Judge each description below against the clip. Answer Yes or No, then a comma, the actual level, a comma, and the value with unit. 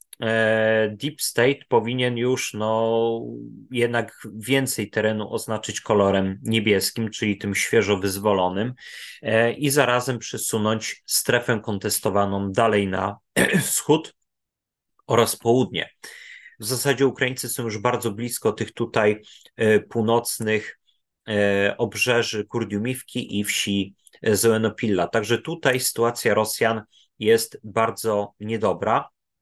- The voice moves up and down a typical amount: No, narrow, 2.3 semitones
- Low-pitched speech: Yes, low, 110 Hz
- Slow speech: Yes, slow, 95 wpm